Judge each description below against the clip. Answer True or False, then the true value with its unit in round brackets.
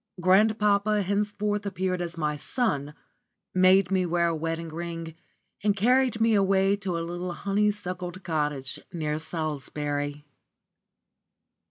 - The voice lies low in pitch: False (180 Hz)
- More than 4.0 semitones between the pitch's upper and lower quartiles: False (3.7 semitones)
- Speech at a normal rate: False (125 wpm)